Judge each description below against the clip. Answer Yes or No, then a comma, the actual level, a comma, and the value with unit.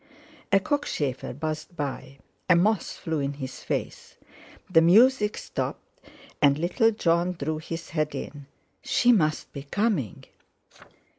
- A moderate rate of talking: No, slow, 130 wpm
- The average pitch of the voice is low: No, medium, 165 Hz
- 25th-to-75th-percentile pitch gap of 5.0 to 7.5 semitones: Yes, wide, 5.5 semitones